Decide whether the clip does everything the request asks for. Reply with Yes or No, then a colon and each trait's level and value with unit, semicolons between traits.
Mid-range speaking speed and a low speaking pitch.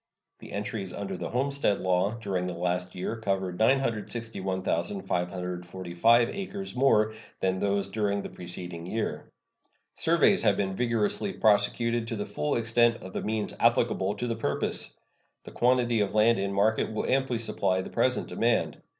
Yes: average, 150 wpm; low, 105 Hz